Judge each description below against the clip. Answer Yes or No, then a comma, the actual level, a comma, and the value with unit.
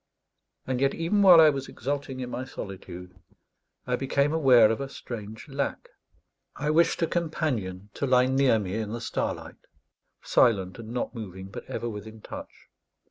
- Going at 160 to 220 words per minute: Yes, average, 165 wpm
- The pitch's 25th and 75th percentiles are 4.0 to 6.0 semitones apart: Yes, average, 4.6 semitones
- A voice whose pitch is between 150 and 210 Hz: No, low, 125 Hz